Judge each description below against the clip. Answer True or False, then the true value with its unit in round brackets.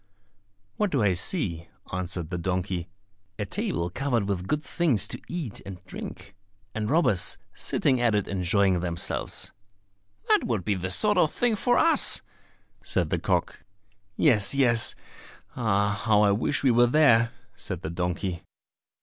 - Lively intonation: True (5.9 semitones)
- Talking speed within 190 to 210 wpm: False (150 wpm)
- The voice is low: True (105 Hz)